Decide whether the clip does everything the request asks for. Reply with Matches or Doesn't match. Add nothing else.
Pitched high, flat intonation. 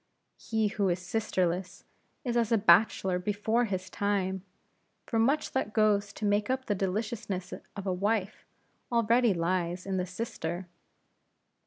Doesn't match